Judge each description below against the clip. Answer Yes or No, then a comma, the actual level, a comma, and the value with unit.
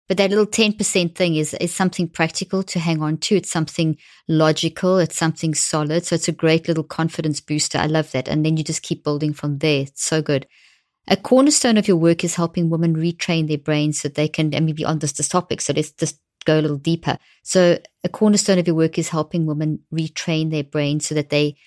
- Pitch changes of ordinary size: No, narrow, 2.3 semitones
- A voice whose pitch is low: No, medium, 160 Hz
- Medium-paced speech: No, fast, 235 wpm